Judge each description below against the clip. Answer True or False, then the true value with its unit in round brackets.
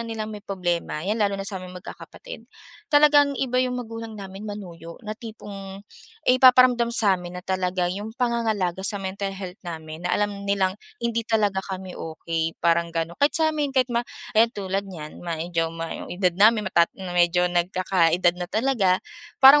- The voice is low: False (195 Hz)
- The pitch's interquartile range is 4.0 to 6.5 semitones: True (4.3 semitones)